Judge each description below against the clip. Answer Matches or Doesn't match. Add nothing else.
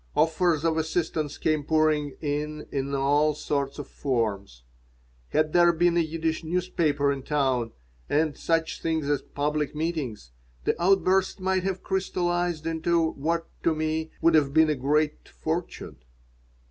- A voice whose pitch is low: Doesn't match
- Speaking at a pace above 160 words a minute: Doesn't match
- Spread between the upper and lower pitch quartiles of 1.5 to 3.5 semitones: Matches